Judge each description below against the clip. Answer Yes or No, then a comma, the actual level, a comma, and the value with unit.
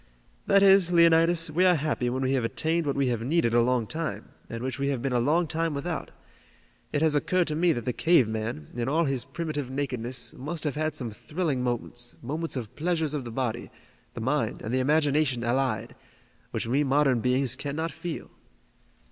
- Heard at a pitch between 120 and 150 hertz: Yes, medium, 140 Hz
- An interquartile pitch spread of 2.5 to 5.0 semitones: Yes, average, 4.7 semitones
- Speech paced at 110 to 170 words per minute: No, average, 200 wpm